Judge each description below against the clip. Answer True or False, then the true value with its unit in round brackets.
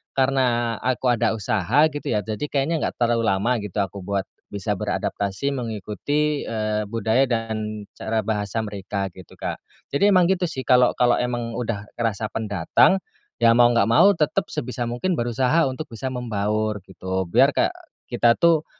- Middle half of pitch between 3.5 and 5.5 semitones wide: True (3.8 semitones)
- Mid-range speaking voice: False (115 Hz)